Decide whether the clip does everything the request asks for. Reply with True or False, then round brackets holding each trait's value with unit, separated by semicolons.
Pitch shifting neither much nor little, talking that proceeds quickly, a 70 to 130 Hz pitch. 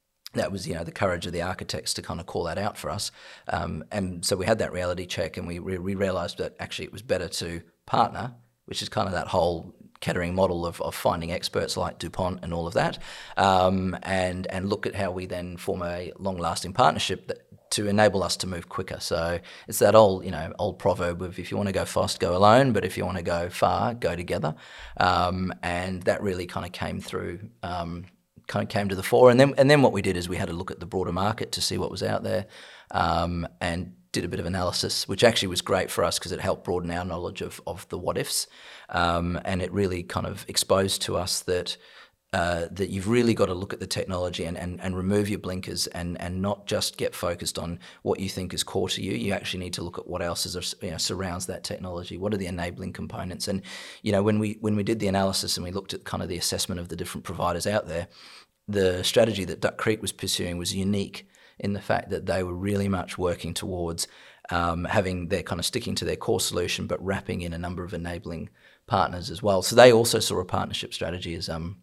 False (2.1 semitones; 245 wpm; 90 Hz)